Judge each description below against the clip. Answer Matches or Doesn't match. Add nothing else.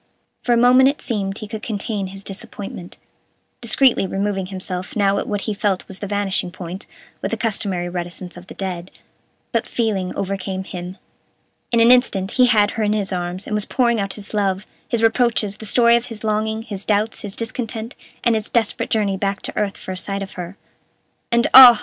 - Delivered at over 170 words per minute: Matches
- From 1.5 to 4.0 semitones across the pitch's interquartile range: Matches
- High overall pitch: Matches